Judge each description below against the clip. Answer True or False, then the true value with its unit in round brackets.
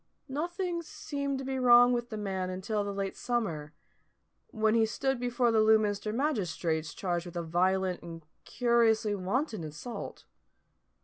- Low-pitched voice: False (220 Hz)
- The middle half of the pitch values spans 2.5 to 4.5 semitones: False (5.0 semitones)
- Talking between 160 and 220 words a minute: False (145 wpm)